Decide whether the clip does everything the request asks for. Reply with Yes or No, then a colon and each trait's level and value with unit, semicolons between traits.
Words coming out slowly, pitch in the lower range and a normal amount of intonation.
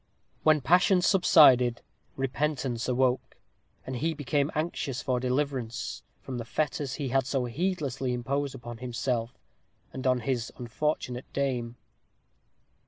Yes: slow, 120 wpm; low, 130 Hz; average, 3.0 semitones